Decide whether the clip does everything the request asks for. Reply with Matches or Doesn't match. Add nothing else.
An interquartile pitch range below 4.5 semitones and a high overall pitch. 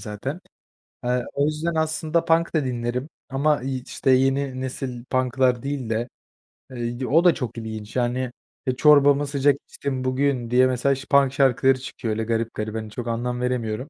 Doesn't match